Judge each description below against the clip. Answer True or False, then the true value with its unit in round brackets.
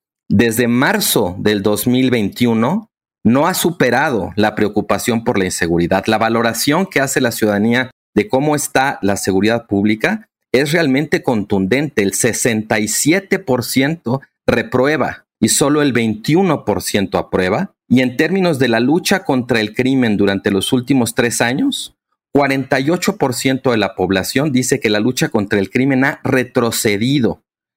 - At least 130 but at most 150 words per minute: True (135 wpm)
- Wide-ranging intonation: False (4.7 semitones)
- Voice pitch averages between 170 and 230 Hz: False (125 Hz)